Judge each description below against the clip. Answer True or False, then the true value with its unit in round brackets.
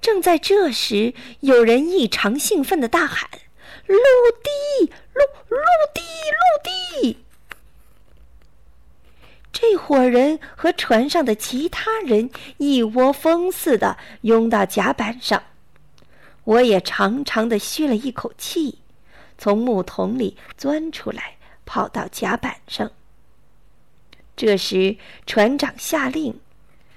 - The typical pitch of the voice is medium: False (275 Hz)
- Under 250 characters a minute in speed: True (150 characters per minute)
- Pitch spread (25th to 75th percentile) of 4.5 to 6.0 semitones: False (6.7 semitones)